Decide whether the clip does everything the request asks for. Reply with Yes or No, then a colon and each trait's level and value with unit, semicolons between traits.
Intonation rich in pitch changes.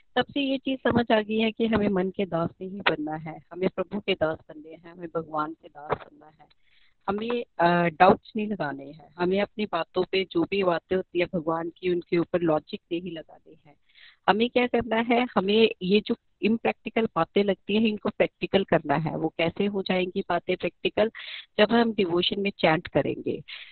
No: average, 4.2 semitones